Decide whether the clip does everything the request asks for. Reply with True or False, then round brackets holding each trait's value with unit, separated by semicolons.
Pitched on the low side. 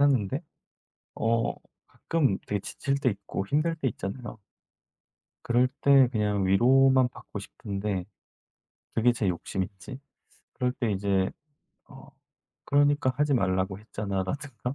True (115 Hz)